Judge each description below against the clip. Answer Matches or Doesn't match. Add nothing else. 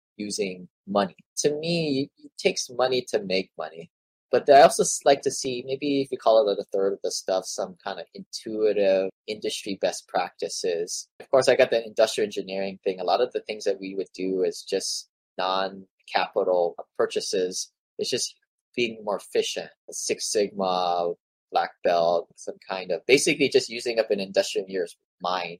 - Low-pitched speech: Doesn't match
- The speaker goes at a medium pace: Matches